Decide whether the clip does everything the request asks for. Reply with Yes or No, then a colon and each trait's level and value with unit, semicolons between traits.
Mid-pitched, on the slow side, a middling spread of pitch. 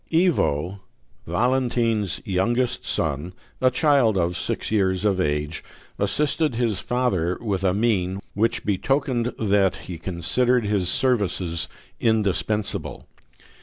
No: low, 100 Hz; slow, 110 wpm; average, 5.0 semitones